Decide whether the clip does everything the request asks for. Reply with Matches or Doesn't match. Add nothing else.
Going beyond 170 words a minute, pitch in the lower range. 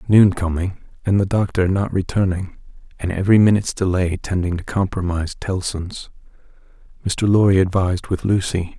Doesn't match